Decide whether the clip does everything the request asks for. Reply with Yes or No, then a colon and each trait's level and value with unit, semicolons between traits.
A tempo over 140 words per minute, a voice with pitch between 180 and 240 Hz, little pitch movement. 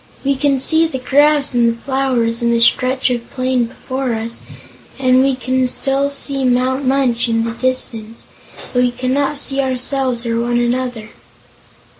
No: average, 165 wpm; very high, 255 Hz; narrow, 2.2 semitones